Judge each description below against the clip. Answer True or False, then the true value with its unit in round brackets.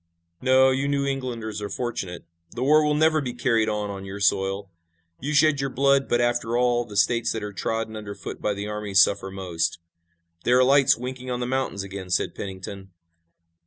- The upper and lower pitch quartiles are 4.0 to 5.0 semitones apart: True (4.7 semitones)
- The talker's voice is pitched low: True (115 Hz)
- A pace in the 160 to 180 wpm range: False (200 wpm)